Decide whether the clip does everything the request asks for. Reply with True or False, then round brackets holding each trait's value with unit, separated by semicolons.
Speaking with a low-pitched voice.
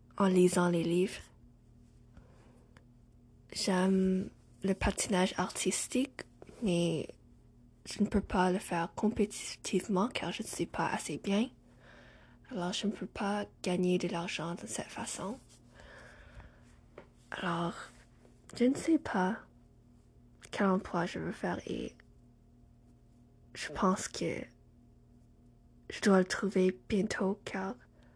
False (180 Hz)